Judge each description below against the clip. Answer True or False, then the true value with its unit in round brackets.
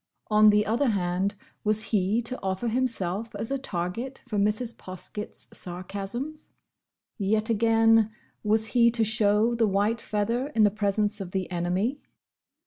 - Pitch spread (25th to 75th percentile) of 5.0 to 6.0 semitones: False (2.7 semitones)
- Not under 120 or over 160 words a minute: True (145 wpm)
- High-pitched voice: True (215 Hz)